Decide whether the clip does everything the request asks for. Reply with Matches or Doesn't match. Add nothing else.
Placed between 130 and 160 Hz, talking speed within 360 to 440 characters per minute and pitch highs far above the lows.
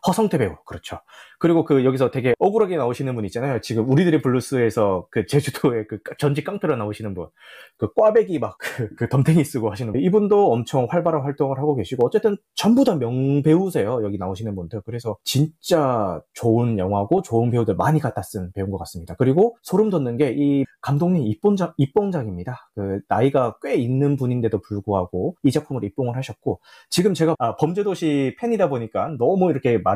Matches